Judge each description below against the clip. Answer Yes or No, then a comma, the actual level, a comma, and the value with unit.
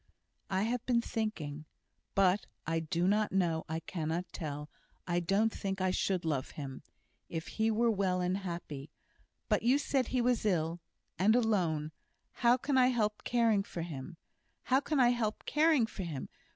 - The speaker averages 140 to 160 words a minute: No, average, 170 wpm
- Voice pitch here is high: Yes, high, 195 Hz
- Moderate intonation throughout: No, wide, 5.9 semitones